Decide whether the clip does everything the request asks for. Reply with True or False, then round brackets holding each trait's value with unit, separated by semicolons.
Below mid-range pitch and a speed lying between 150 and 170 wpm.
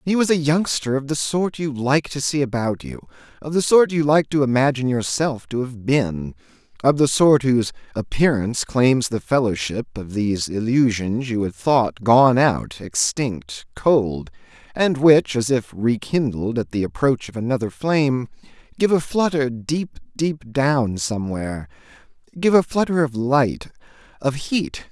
True (125 Hz; 160 wpm)